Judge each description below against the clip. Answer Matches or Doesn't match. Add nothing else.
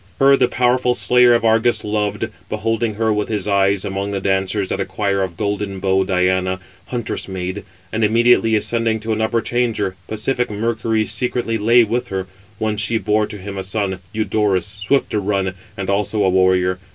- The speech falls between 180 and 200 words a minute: Matches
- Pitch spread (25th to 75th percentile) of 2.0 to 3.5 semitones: Matches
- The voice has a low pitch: Matches